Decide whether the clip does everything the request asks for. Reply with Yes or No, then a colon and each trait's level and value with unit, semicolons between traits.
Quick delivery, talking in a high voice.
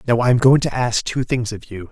No: fast, 315 wpm; low, 120 Hz